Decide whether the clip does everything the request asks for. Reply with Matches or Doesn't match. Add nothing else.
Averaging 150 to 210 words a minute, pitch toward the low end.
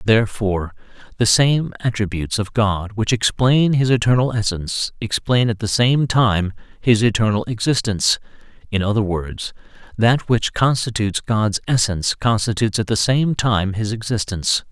Doesn't match